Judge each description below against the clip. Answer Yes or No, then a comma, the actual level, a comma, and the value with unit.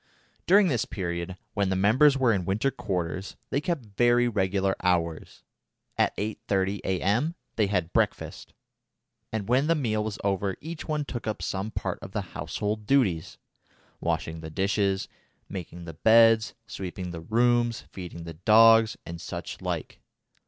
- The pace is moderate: Yes, average, 150 wpm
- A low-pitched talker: Yes, low, 105 Hz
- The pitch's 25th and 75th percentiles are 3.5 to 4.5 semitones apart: Yes, average, 4.1 semitones